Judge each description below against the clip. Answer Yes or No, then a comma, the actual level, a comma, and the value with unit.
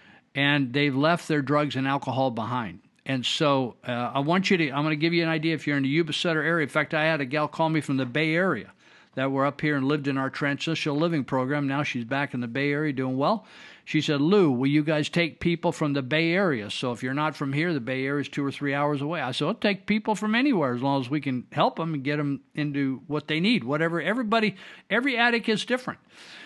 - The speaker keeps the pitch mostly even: No, average, 3.3 semitones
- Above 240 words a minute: Yes, fast, 255 wpm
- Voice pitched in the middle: Yes, medium, 150 Hz